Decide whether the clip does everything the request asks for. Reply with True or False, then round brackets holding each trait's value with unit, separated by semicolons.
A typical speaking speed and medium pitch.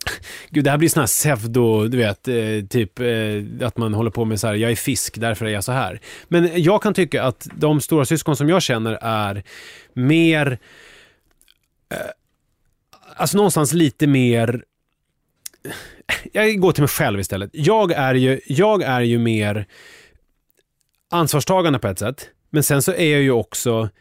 False (165 wpm; 130 Hz)